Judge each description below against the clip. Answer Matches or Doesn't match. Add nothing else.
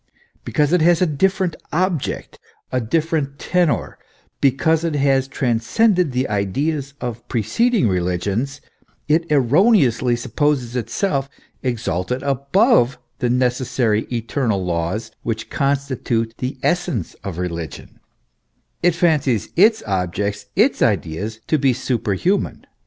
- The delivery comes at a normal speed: Doesn't match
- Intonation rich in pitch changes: Matches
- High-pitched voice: Doesn't match